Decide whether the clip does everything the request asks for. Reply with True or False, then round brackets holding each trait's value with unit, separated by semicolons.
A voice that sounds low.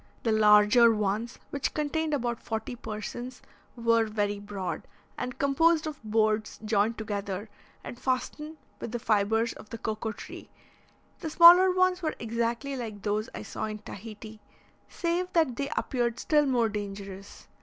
False (230 Hz)